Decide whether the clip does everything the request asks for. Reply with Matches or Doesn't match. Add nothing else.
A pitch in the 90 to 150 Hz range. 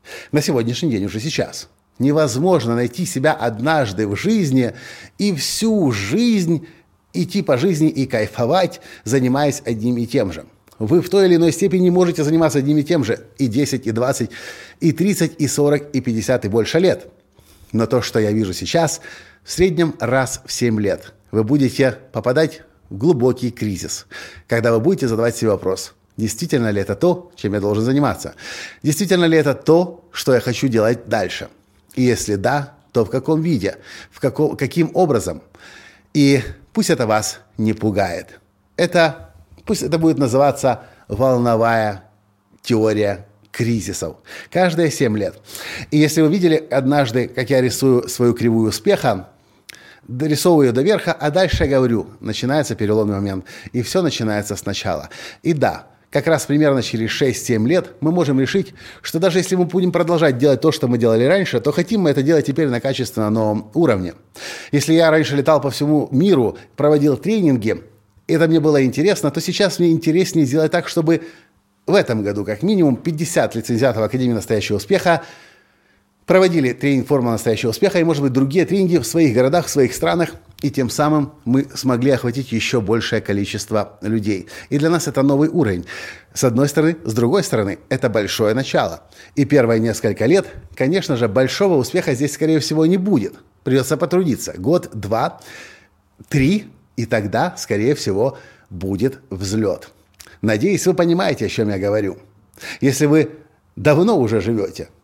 Matches